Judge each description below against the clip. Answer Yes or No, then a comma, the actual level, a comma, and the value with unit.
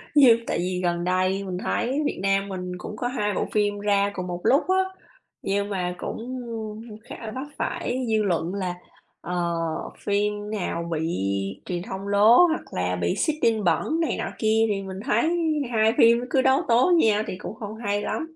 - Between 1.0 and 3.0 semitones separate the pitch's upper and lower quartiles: No, average, 4.1 semitones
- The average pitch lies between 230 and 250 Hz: No, high, 205 Hz